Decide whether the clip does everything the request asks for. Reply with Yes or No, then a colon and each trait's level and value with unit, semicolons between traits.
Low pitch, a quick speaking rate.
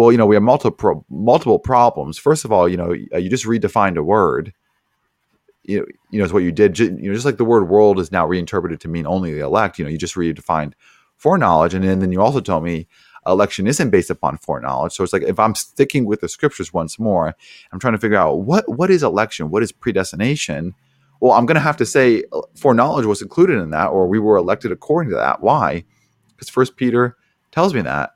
Yes: low, 105 Hz; fast, 230 wpm